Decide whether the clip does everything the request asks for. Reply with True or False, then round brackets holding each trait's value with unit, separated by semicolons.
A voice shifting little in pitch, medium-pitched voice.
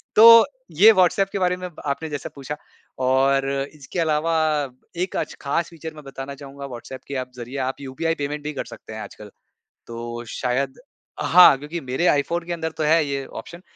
False (3.8 semitones; 145 Hz)